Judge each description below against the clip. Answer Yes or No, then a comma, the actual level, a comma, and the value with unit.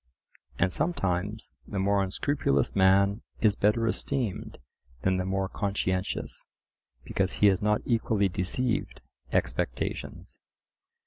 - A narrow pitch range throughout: Yes, narrow, 2.3 semitones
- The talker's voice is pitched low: Yes, low, 100 Hz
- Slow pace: Yes, slow, 110 wpm